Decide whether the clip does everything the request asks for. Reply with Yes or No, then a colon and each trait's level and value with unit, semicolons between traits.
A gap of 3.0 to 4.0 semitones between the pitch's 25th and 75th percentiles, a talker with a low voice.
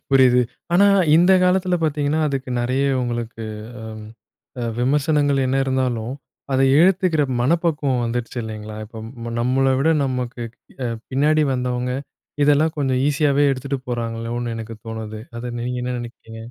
Yes: average, 3.5 semitones; low, 130 Hz